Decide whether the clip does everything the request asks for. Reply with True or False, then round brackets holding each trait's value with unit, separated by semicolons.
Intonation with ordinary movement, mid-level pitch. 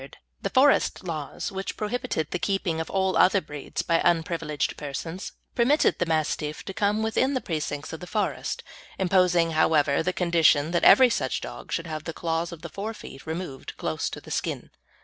True (3.6 semitones; 170 Hz)